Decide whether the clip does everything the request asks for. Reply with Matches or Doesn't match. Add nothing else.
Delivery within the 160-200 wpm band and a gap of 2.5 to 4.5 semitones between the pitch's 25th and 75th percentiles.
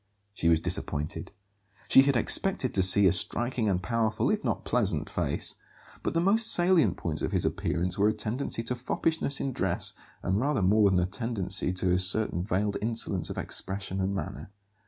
Doesn't match